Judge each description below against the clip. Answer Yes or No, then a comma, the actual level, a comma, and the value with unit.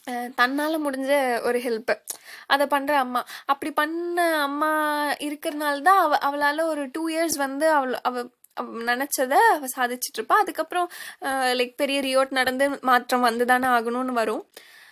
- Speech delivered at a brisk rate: Yes, fast, 135 wpm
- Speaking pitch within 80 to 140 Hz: No, very high, 280 Hz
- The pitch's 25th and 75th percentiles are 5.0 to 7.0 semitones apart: No, average, 4.0 semitones